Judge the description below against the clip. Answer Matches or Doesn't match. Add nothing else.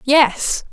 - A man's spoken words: Doesn't match